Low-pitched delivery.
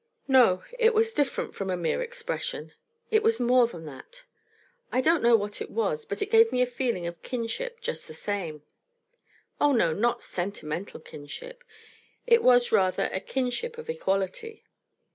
No: very high, 250 Hz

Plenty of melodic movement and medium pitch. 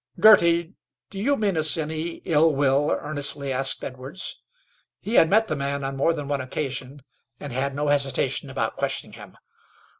No: average, 3.4 semitones; medium, 145 Hz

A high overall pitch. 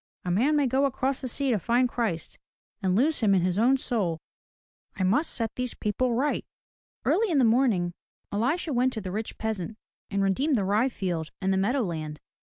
Yes: high, 225 Hz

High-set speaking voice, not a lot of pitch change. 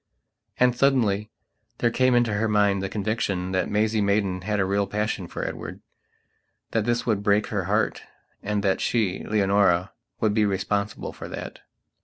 No: low, 105 Hz; narrow, 2.0 semitones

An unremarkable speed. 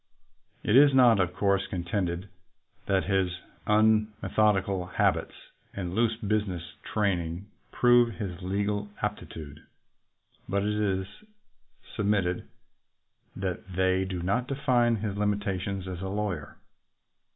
No: slow, 115 wpm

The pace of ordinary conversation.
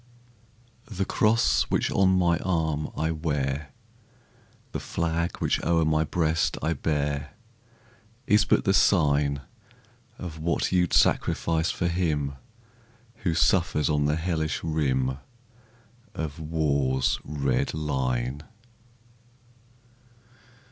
No: slow, 105 wpm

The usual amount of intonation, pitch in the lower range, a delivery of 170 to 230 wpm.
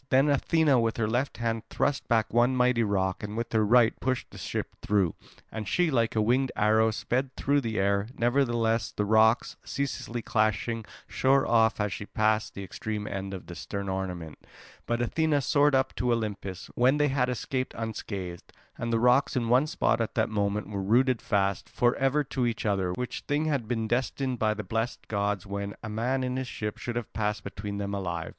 Yes: average, 3.5 semitones; low, 115 Hz; average, 200 wpm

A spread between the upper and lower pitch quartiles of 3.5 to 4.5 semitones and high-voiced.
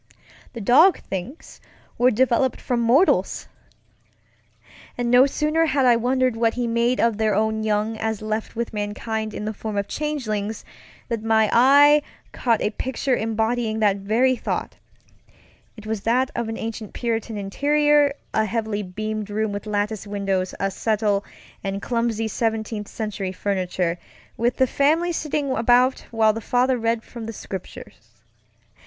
No: average, 2.8 semitones; high, 225 Hz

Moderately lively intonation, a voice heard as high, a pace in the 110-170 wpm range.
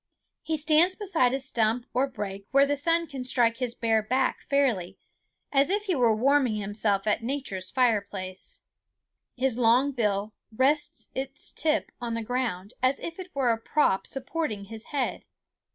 Yes: average, 4.4 semitones; very high, 250 Hz; average, 165 wpm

